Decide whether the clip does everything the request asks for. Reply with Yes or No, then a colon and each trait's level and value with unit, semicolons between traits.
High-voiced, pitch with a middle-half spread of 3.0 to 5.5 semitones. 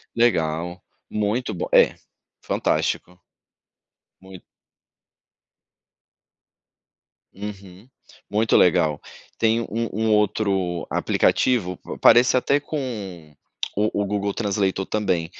No: low, 100 Hz; average, 3.7 semitones